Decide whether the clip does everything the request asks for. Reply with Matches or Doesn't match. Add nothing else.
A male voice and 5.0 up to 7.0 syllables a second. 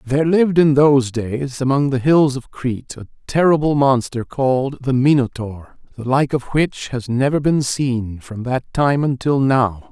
Doesn't match